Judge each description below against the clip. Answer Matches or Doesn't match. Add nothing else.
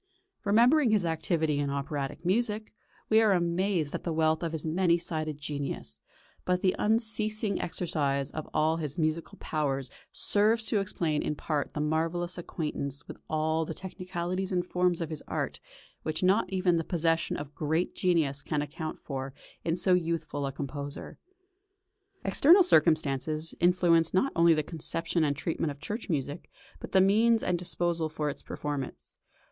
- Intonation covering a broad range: Doesn't match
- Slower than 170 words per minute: Matches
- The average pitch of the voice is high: Doesn't match